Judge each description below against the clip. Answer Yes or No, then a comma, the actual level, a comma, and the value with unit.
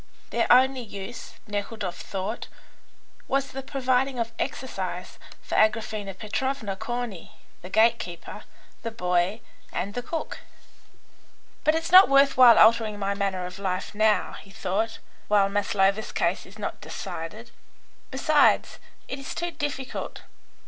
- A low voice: No, high, 220 Hz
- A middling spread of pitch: Yes, average, 4.7 semitones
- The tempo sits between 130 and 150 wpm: Yes, slow, 135 wpm